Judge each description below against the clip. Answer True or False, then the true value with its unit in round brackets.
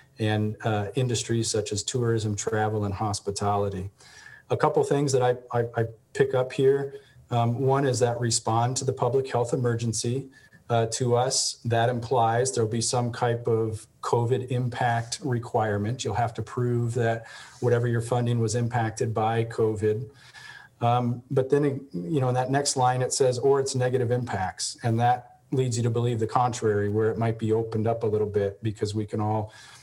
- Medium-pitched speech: False (120 Hz)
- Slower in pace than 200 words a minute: True (185 wpm)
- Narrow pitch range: True (2.3 semitones)